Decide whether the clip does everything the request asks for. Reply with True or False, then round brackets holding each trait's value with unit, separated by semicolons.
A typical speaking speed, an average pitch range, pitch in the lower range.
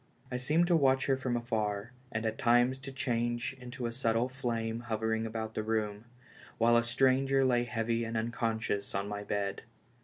False (180 wpm; 2.3 semitones; 115 Hz)